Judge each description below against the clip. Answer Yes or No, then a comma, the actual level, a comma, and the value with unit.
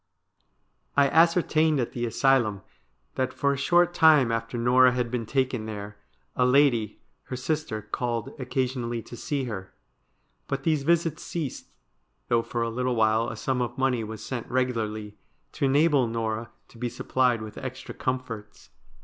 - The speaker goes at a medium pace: Yes, average, 165 wpm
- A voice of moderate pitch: No, low, 125 Hz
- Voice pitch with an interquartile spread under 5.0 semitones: Yes, average, 3.0 semitones